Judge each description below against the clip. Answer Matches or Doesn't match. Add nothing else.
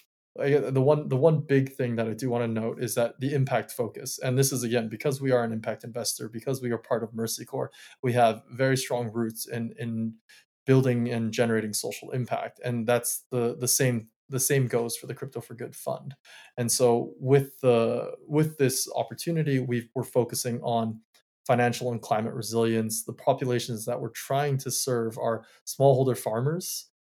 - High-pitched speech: Doesn't match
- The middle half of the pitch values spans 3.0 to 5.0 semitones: Doesn't match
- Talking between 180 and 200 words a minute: Matches